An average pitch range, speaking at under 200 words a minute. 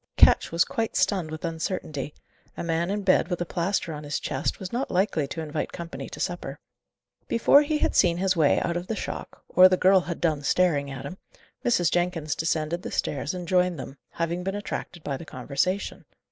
No: average, 3.1 semitones; fast, 205 wpm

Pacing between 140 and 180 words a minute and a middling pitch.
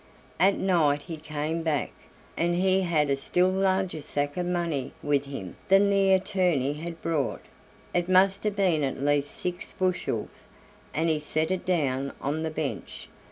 Yes: average, 165 wpm; medium, 165 Hz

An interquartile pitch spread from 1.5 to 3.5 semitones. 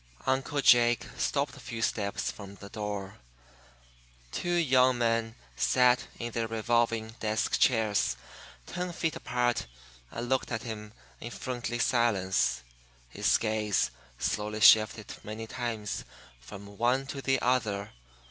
Yes: average, 2.9 semitones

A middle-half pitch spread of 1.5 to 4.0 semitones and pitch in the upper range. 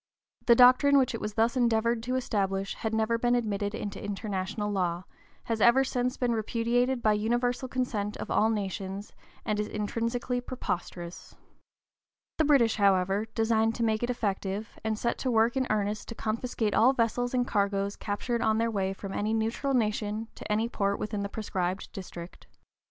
Yes: average, 2.9 semitones; high, 220 Hz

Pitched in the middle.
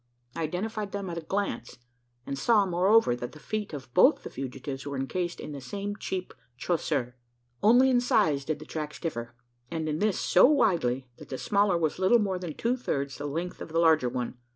Yes: medium, 165 Hz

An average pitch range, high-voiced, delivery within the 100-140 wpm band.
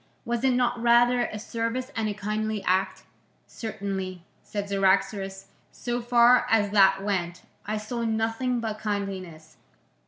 Yes: average, 3.4 semitones; high, 215 Hz; slow, 135 wpm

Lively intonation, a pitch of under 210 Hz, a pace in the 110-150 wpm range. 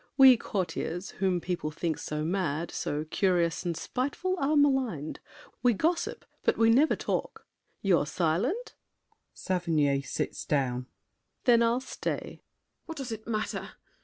Yes: wide, 7.8 semitones; high, 190 Hz; slow, 135 wpm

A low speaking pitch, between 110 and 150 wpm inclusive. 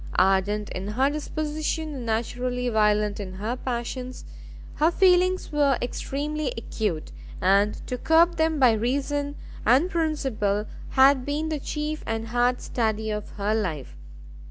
No: very high, 250 Hz; slow, 135 wpm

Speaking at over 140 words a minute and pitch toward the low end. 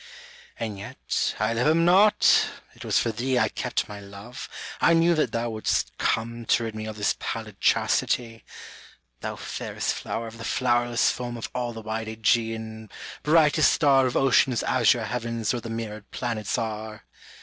Yes: average, 170 wpm; low, 115 Hz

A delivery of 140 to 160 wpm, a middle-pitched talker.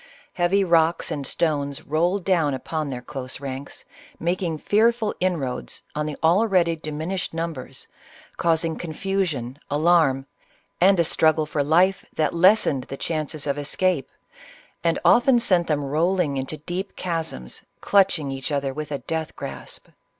Yes: average, 145 wpm; medium, 160 Hz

